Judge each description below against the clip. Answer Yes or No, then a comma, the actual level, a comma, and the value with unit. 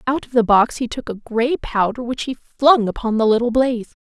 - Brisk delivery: Yes, fast, 235 wpm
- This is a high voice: Yes, high, 235 Hz